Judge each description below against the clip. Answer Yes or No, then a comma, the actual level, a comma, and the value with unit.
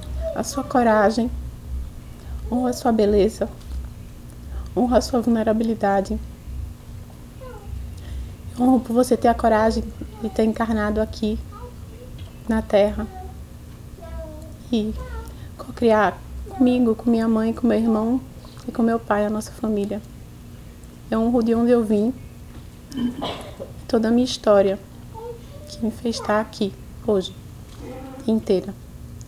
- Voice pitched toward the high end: Yes, high, 220 Hz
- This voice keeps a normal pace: No, slow, 115 wpm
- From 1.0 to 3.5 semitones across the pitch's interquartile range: Yes, average, 2.8 semitones